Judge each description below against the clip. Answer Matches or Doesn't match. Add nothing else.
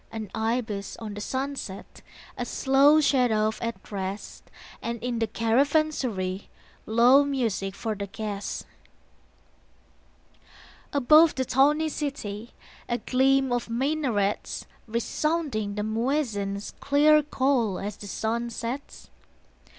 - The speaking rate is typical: Doesn't match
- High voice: Matches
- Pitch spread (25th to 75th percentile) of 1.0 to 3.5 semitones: Doesn't match